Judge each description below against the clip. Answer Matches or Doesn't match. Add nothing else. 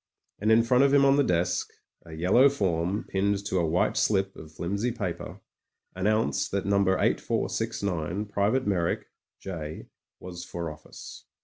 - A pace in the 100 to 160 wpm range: Matches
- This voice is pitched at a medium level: Doesn't match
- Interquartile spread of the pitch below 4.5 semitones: Matches